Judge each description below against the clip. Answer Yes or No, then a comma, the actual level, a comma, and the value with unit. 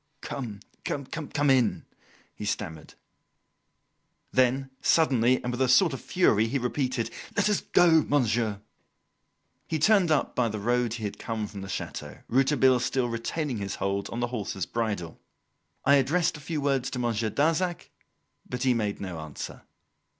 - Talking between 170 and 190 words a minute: No, average, 155 wpm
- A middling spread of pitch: Yes, average, 4.5 semitones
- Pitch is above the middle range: No, low, 125 Hz